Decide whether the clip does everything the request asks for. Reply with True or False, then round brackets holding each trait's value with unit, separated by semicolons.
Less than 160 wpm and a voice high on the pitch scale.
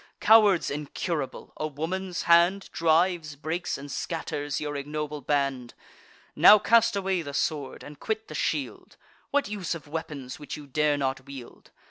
False (150 wpm; 155 Hz)